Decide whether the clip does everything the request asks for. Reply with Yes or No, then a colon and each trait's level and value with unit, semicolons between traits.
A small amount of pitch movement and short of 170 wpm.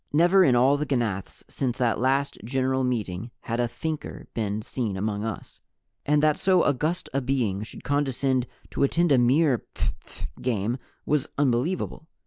No: average, 3.9 semitones; average, 160 wpm